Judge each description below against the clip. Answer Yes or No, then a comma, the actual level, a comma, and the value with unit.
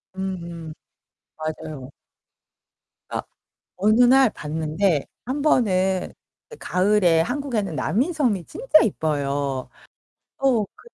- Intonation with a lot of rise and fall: Yes, wide, 7.3 semitones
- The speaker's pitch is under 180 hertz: No, high, 190 Hz